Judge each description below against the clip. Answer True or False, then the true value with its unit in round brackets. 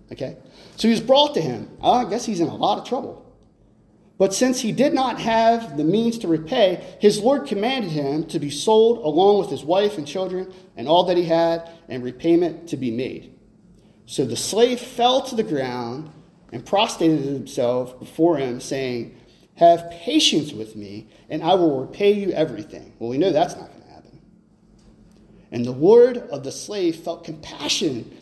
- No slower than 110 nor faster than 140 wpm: False (185 wpm)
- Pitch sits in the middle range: True (170 Hz)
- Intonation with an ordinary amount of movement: False (7.3 semitones)